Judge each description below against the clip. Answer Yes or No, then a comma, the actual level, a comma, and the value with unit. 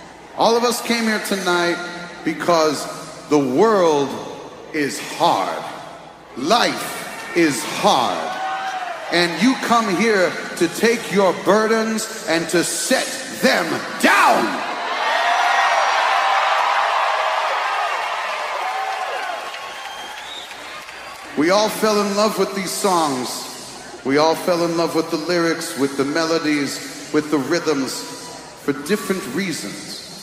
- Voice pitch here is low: No, medium, 175 Hz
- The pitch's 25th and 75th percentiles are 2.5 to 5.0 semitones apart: No, wide, 5.4 semitones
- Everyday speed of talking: No, slow, 105 wpm